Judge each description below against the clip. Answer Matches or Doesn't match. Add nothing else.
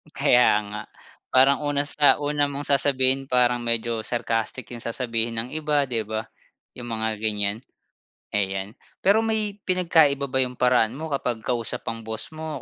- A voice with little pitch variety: Doesn't match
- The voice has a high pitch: Doesn't match